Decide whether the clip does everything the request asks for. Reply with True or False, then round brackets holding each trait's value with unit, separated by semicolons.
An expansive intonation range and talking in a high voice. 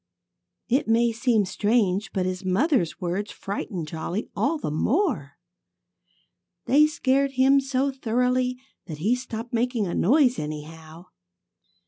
True (6.1 semitones; 230 Hz)